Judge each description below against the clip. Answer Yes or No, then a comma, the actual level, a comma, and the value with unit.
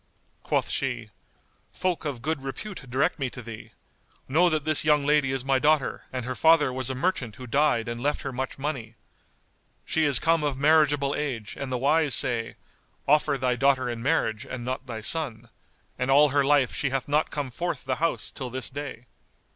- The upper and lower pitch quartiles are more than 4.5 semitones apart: No, average, 2.9 semitones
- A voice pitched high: No, low, 135 Hz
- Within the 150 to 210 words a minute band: Yes, average, 195 wpm